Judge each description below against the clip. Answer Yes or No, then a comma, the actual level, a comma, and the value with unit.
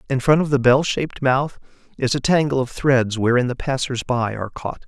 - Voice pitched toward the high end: No, low, 130 Hz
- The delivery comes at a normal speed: No, fast, 220 wpm